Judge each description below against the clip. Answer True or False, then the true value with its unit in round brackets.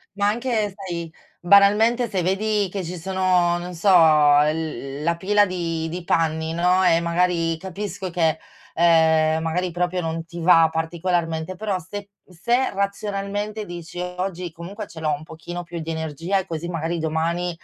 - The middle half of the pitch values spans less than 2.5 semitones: False (2.8 semitones)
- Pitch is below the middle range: False (175 Hz)